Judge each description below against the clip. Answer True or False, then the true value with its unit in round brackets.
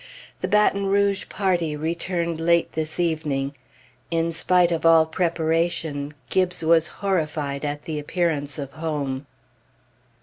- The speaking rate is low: True (125 wpm)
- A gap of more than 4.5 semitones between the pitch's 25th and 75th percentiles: False (2.5 semitones)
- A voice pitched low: False (165 Hz)